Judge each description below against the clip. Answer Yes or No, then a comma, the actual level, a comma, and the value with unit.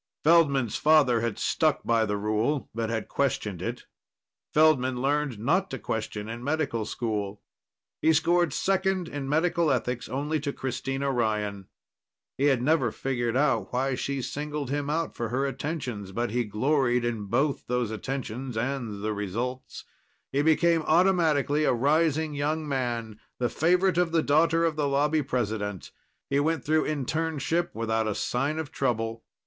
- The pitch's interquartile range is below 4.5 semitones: No, average, 5.0 semitones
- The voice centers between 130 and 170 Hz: Yes, low, 135 Hz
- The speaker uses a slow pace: No, average, 155 wpm